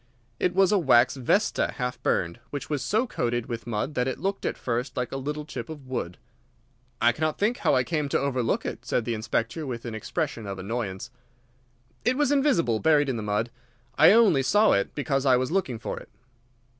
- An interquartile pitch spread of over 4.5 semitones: Yes, average, 5.2 semitones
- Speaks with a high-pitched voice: No, low, 130 Hz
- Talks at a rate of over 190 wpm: Yes, fast, 205 wpm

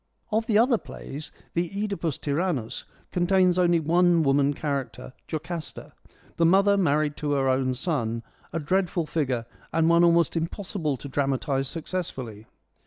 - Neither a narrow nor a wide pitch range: Yes, average, 4.4 semitones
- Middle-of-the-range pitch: Yes, medium, 160 Hz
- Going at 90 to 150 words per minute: Yes, average, 145 wpm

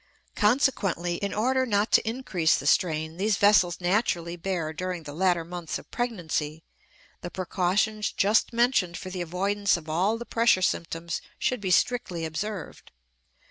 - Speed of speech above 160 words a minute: No, average, 150 wpm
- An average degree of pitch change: Yes, average, 3.9 semitones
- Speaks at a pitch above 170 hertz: Yes, medium, 185 Hz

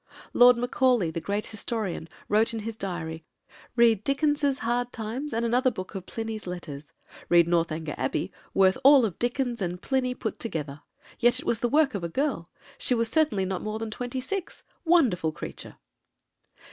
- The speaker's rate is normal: Yes, average, 170 wpm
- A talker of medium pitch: No, high, 225 Hz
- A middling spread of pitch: No, wide, 5.7 semitones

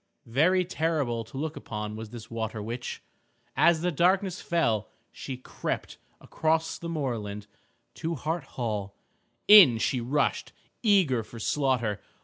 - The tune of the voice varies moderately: No, wide, 6.6 semitones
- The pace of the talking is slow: Yes, slow, 130 wpm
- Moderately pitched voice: No, low, 130 Hz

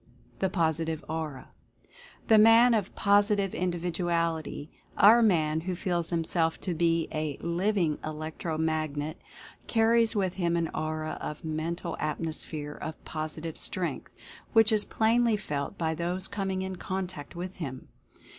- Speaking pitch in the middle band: Yes, medium, 170 Hz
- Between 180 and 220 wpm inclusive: No, average, 145 wpm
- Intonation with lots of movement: No, average, 3.5 semitones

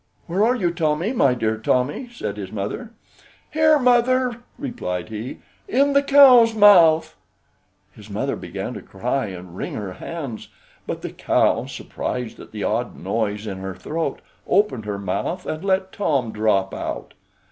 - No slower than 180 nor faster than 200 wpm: No, average, 160 wpm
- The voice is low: No, medium, 150 Hz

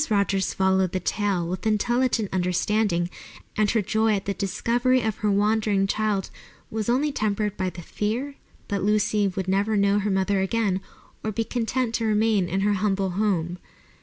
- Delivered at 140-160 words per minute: No, average, 170 wpm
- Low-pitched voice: No, high, 205 Hz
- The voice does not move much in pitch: Yes, narrow, 2.3 semitones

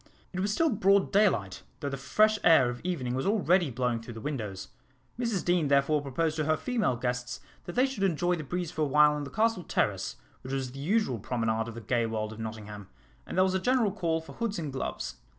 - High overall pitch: No, medium, 150 Hz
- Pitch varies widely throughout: Yes, wide, 7.4 semitones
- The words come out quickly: Yes, fast, 230 wpm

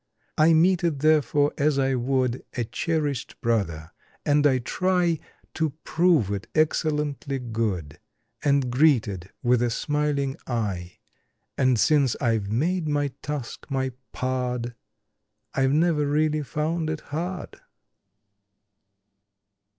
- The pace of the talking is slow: Yes, slow, 120 wpm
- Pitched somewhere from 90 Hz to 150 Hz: Yes, medium, 140 Hz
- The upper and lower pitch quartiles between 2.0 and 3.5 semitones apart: No, average, 4.2 semitones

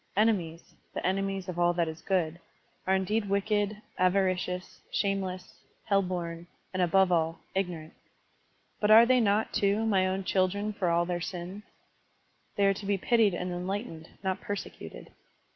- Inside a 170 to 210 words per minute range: No, average, 160 wpm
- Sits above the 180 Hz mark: Yes, high, 190 Hz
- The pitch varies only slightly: Yes, narrow, 2.3 semitones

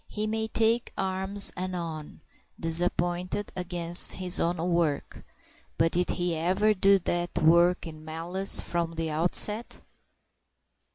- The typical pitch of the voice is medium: Yes, medium, 175 Hz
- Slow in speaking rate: Yes, slow, 120 wpm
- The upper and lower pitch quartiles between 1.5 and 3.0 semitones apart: Yes, narrow, 2.4 semitones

